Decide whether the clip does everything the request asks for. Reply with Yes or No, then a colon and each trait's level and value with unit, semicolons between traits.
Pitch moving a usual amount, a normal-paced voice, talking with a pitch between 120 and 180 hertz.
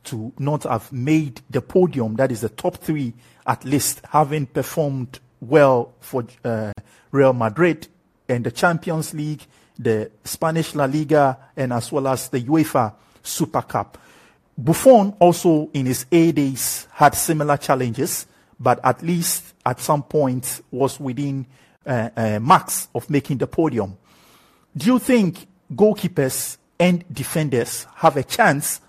Yes: average, 4.3 semitones; average, 145 wpm; medium, 140 Hz